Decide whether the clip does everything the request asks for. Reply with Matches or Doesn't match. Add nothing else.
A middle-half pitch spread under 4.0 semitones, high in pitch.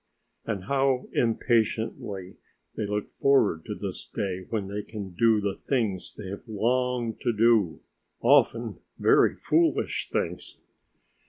Doesn't match